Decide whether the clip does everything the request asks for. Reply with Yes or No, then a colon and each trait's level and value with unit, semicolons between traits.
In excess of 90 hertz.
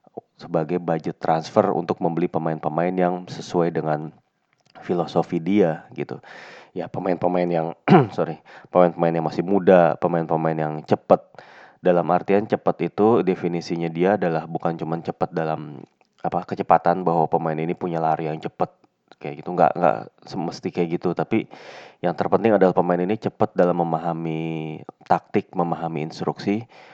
No: very low, 85 Hz